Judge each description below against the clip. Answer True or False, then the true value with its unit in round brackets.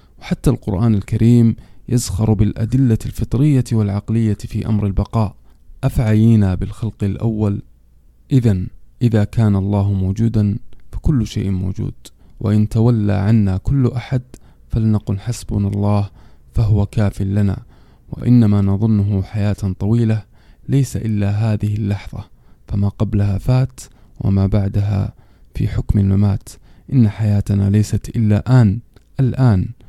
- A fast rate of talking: False (110 wpm)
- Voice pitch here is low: True (105 Hz)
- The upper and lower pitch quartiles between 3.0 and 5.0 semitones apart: False (2.5 semitones)